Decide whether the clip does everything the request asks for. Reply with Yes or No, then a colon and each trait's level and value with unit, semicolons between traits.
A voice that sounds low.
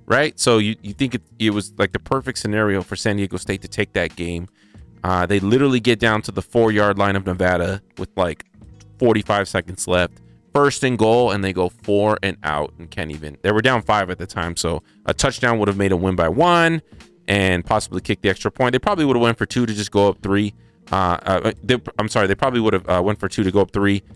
Yes: low, 105 Hz